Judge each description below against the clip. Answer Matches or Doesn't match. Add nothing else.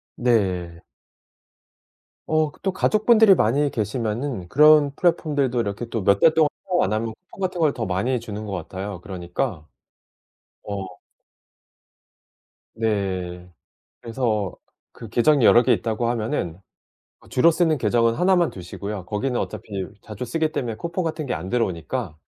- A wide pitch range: Matches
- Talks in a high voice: Doesn't match